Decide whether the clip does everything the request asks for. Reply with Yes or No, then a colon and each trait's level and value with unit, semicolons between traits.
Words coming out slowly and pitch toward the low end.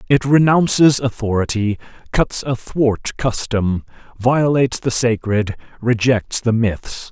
Yes: slow, 100 wpm; low, 120 Hz